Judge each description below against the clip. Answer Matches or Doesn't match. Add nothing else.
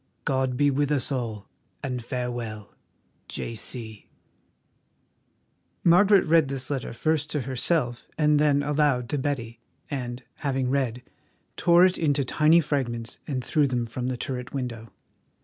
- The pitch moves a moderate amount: Matches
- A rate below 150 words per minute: Matches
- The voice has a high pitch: Doesn't match